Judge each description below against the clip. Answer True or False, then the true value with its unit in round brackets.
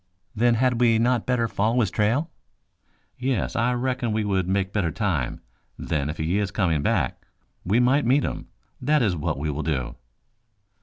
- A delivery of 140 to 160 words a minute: False (175 wpm)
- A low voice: True (110 Hz)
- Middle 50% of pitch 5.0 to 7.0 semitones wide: True (5.6 semitones)